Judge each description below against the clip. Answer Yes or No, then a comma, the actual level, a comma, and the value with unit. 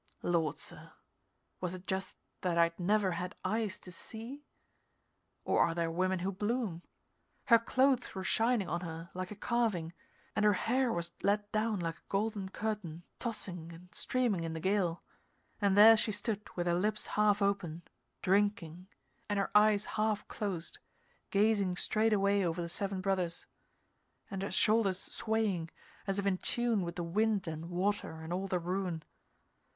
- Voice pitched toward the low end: No, high, 195 Hz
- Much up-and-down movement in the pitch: No, average, 3.5 semitones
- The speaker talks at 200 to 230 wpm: No, average, 165 wpm